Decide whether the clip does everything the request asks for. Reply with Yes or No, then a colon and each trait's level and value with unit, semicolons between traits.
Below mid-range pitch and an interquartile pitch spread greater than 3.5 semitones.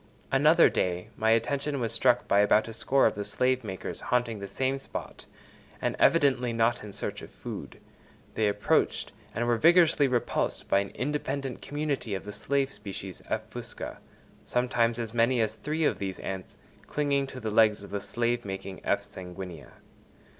Yes: low, 115 Hz; average, 4.8 semitones